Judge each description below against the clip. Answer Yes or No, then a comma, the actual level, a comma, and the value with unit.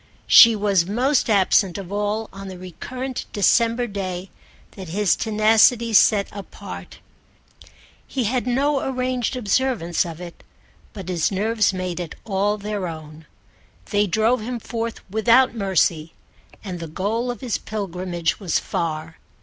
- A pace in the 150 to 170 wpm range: No, average, 140 wpm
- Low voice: No, high, 205 Hz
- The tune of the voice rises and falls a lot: No, average, 4.2 semitones